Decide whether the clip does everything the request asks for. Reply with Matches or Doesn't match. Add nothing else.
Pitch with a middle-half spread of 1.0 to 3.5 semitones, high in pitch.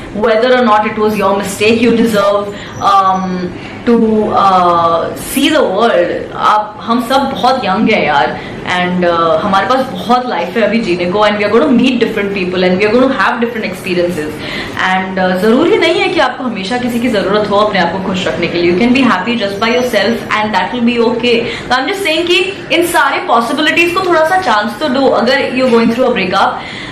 Doesn't match